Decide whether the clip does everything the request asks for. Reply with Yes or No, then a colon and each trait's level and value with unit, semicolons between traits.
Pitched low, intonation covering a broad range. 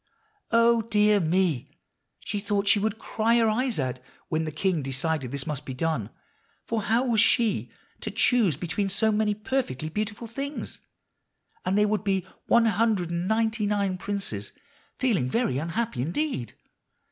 No: high, 205 Hz; wide, 5.8 semitones